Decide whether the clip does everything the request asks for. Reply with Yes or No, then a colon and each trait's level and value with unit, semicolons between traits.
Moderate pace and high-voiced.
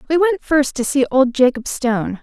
No: fast, 215 wpm; very high, 275 Hz